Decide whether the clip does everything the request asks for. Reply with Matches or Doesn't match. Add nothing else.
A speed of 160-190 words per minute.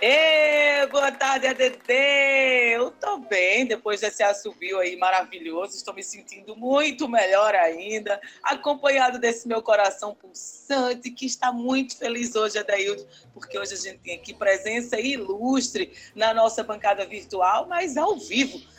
Doesn't match